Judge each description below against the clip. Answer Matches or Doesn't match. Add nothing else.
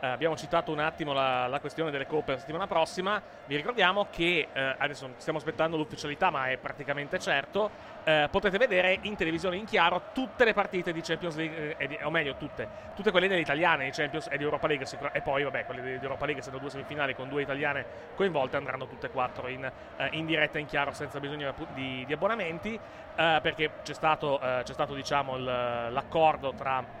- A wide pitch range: Doesn't match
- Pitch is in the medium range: Matches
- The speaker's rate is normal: Doesn't match